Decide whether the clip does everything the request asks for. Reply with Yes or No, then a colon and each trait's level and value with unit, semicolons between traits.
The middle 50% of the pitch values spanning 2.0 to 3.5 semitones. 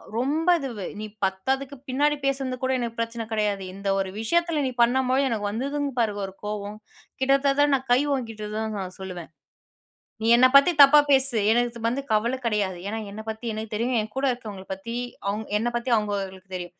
No: average, 4.2 semitones